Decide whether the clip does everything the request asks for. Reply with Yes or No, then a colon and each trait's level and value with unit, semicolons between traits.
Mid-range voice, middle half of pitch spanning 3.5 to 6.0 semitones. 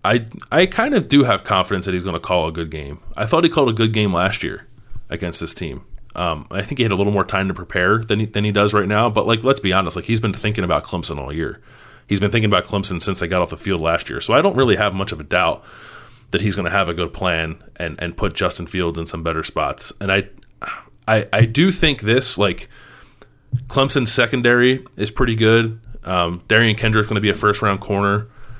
No: low, 100 Hz; average, 4.2 semitones